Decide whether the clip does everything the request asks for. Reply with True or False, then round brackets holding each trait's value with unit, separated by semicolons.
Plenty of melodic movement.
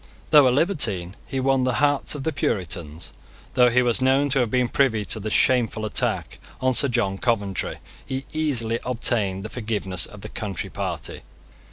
False (4.0 semitones)